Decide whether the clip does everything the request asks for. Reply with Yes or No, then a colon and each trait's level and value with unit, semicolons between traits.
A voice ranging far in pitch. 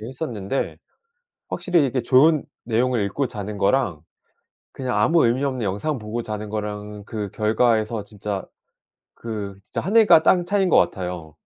No: average, 4.6 semitones